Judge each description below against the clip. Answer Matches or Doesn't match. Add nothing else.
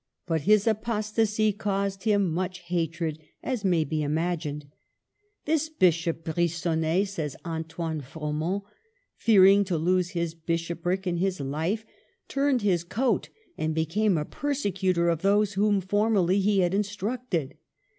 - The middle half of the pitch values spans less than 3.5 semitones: Doesn't match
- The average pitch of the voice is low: Doesn't match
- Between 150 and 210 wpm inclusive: Doesn't match